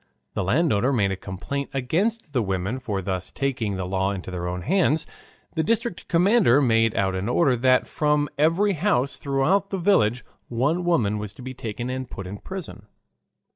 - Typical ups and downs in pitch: No, wide, 8.2 semitones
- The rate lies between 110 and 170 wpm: No, average, 180 wpm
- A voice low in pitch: Yes, low, 130 Hz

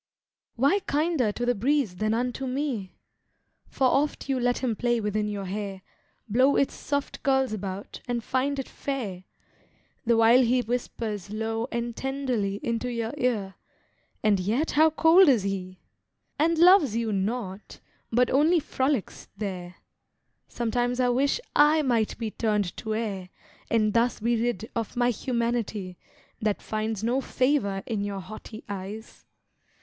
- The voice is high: Yes, high, 235 Hz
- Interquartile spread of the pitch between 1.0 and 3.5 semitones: No, average, 3.9 semitones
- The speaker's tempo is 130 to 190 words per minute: Yes, average, 150 wpm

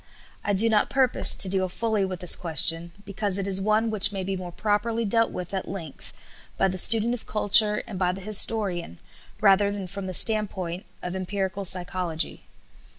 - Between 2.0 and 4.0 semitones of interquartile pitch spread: Yes, narrow, 2.6 semitones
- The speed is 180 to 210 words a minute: Yes, average, 185 wpm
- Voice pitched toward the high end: Yes, high, 195 Hz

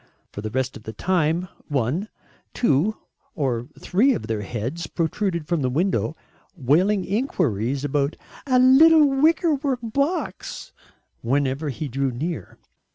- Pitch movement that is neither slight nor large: No, wide, 8.7 semitones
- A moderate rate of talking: No, slow, 130 wpm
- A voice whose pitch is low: No, medium, 160 Hz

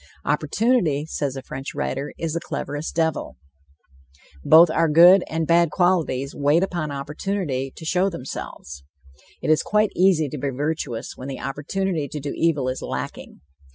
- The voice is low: No, medium, 155 Hz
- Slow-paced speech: No, average, 155 wpm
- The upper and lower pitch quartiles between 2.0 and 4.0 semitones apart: Yes, average, 3.7 semitones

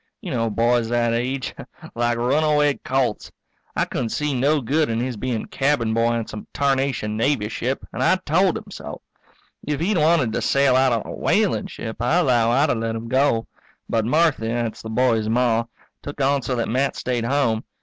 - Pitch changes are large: No, average, 3.5 semitones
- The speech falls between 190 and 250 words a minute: Yes, average, 195 wpm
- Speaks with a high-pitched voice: No, low, 125 Hz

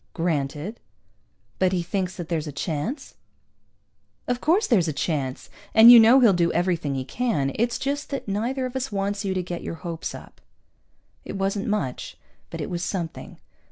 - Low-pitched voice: No, high, 190 Hz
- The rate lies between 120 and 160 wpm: No, average, 180 wpm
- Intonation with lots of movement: Yes, wide, 6.0 semitones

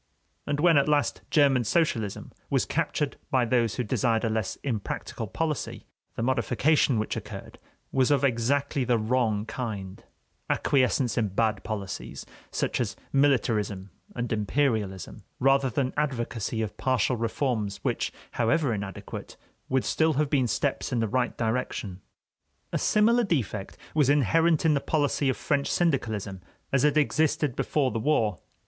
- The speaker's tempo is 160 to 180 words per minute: No, average, 145 wpm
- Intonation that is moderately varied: Yes, average, 4.5 semitones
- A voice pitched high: No, low, 125 Hz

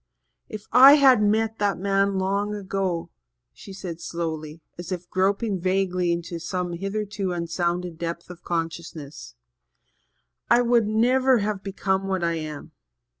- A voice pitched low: No, high, 190 Hz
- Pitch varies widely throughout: No, average, 3.2 semitones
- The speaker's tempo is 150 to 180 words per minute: No, slow, 135 wpm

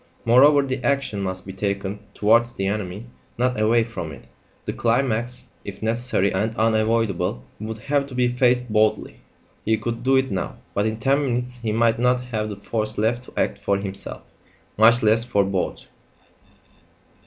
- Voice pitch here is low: Yes, low, 110 Hz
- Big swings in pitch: No, average, 3.2 semitones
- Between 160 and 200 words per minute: Yes, average, 170 wpm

